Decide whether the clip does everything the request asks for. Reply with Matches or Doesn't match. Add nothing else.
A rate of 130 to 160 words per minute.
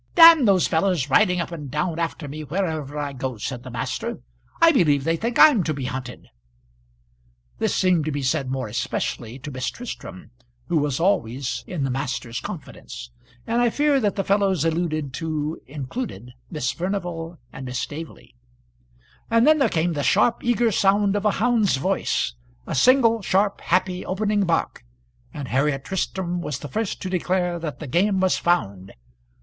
Doesn't match